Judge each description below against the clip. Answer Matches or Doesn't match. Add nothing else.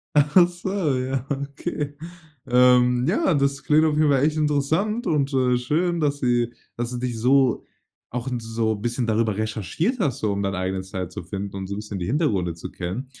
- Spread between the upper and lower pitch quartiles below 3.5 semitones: Doesn't match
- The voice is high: Doesn't match